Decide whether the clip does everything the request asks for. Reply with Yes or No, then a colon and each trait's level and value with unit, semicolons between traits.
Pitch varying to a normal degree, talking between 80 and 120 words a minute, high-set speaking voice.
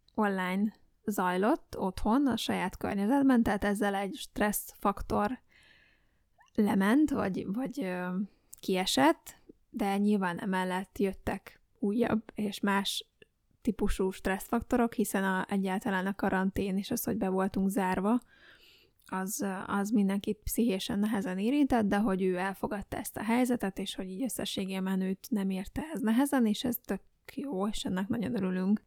No: average, 3.3 semitones; average, 135 wpm; high, 205 Hz